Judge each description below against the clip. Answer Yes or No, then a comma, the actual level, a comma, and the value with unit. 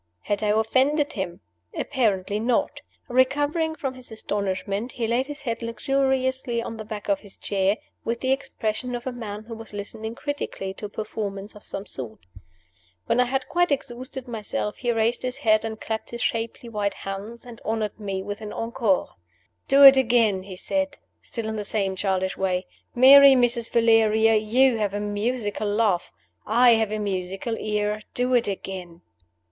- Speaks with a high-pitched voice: Yes, high, 225 Hz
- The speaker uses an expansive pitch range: No, average, 3.4 semitones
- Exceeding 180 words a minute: No, average, 175 wpm